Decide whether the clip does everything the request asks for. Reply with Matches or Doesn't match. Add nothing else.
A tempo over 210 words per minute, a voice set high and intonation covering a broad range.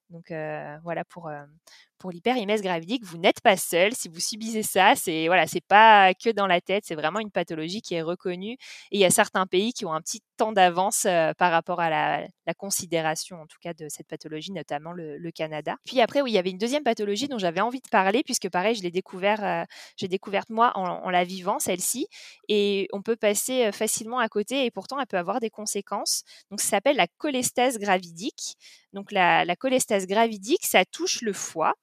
Doesn't match